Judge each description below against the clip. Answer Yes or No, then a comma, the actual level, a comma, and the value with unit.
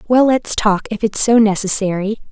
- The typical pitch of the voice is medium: No, high, 215 Hz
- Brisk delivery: No, average, 180 wpm